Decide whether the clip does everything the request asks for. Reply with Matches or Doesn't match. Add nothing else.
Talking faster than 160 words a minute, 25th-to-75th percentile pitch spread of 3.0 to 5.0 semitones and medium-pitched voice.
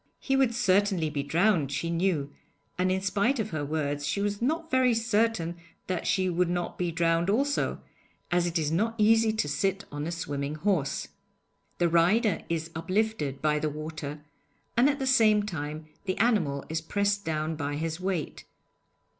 Doesn't match